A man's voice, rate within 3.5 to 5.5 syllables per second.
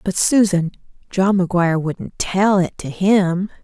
No: female; 4.2 syllables/s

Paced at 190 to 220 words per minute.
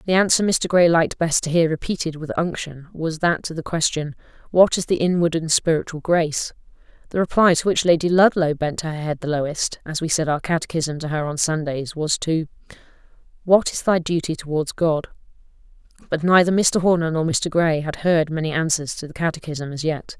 Yes: average, 200 wpm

